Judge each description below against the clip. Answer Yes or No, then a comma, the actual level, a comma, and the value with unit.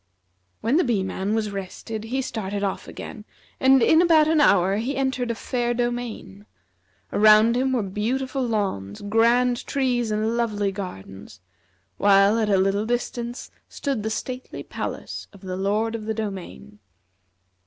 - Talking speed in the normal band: Yes, average, 155 wpm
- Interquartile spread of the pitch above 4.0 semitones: No, average, 3.7 semitones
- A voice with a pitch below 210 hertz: No, high, 220 Hz